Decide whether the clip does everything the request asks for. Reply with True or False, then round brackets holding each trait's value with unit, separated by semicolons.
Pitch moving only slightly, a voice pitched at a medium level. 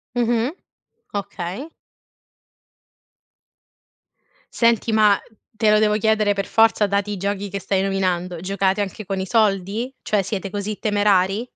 False (2.0 semitones; 205 Hz)